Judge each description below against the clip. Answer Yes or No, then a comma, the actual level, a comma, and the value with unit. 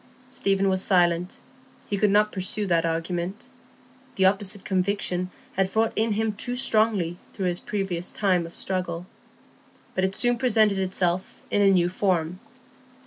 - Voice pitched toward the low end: No, high, 190 Hz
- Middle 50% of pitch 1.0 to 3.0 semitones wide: Yes, average, 2.7 semitones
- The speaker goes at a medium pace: Yes, average, 150 wpm